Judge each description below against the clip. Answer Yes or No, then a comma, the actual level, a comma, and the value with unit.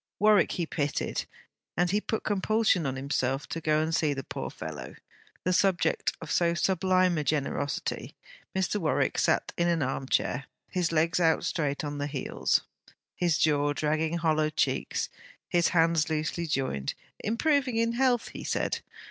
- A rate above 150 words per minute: Yes, average, 160 wpm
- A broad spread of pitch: No, average, 4.0 semitones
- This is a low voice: No, medium, 165 Hz